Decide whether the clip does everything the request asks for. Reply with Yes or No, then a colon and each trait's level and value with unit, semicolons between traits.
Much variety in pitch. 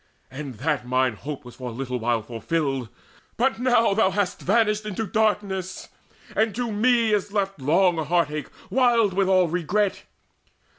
Yes: wide, 7.2 semitones